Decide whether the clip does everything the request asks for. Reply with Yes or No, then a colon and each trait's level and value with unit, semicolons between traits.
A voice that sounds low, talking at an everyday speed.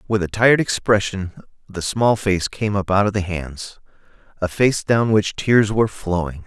Yes: low, 100 Hz; average, 175 wpm